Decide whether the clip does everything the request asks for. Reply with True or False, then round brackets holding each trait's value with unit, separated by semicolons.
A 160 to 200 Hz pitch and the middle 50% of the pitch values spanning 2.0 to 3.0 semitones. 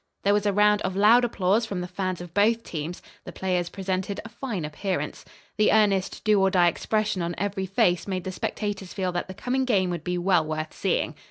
True (190 Hz; 2.6 semitones)